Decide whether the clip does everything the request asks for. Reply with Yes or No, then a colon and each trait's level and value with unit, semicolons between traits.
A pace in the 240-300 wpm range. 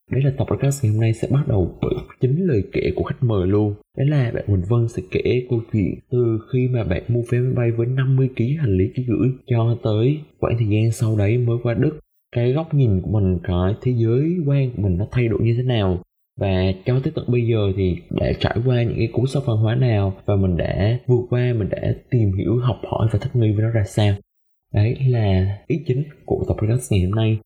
Yes: average, 245 wpm